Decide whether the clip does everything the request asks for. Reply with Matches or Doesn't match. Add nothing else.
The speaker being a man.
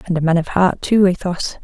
Doesn't match